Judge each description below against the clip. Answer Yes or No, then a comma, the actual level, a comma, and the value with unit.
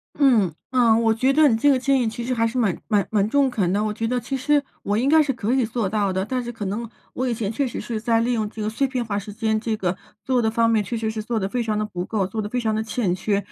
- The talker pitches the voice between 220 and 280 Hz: Yes, high, 225 Hz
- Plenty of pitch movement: No, average, 2.8 semitones